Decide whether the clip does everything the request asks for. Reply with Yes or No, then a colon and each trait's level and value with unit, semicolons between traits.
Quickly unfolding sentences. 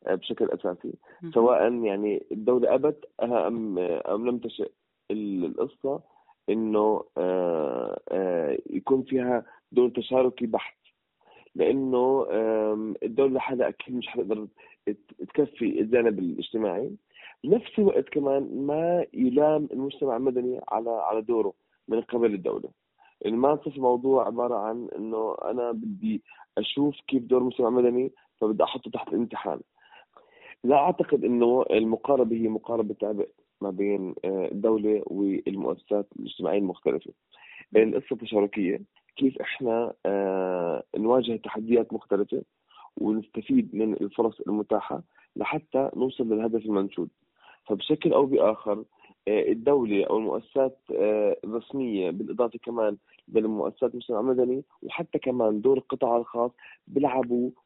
No: average, 105 wpm